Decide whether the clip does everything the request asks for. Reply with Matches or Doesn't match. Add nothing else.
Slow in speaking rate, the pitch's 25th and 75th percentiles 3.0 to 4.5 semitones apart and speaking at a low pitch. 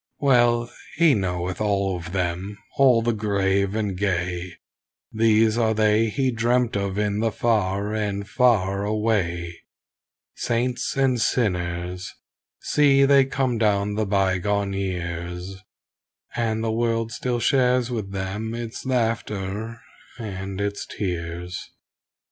Matches